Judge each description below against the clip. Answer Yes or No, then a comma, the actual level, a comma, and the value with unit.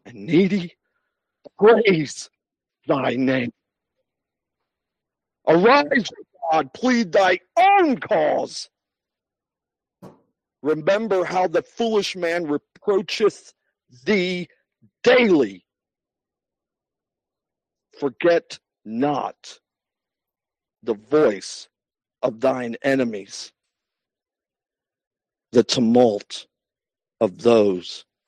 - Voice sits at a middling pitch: Yes, medium, 170 Hz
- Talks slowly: Yes, slow, 65 wpm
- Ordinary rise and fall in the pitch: No, wide, 8.4 semitones